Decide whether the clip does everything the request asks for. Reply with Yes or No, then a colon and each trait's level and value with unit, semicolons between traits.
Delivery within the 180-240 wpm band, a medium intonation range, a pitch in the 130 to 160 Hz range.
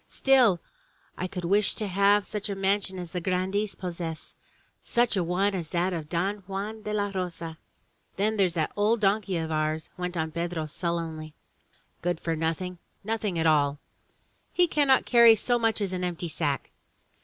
No: average, 185 wpm; average, 3.6 semitones; medium, 185 Hz